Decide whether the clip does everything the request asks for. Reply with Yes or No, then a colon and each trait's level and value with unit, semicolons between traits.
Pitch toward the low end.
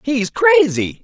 No: medium, 180 Hz